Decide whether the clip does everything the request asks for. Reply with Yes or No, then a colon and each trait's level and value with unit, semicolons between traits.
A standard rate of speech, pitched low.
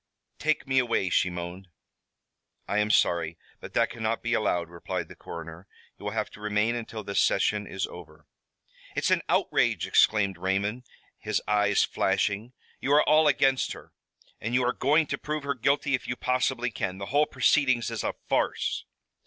Yes: average, 180 wpm; low, 110 Hz